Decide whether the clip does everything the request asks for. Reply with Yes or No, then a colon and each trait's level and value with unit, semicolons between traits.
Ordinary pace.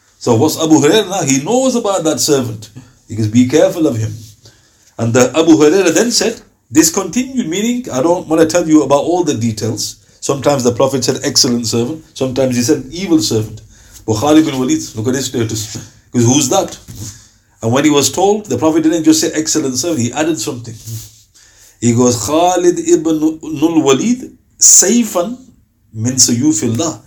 Yes: average, 170 wpm